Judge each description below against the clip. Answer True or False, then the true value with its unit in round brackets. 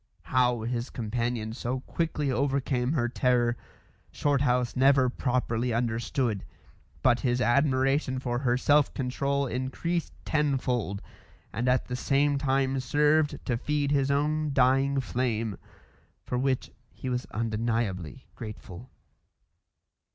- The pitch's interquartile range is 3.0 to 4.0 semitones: False (2.5 semitones)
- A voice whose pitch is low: True (130 Hz)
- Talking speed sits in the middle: False (115 wpm)